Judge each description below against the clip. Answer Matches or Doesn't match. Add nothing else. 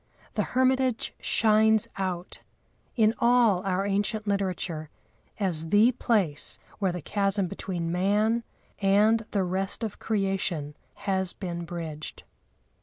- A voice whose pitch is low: Doesn't match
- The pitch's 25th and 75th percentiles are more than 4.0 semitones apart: Doesn't match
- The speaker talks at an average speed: Doesn't match